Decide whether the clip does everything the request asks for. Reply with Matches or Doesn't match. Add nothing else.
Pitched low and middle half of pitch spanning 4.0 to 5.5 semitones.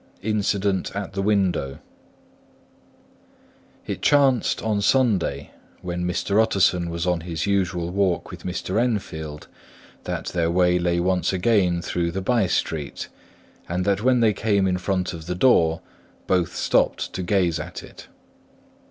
Doesn't match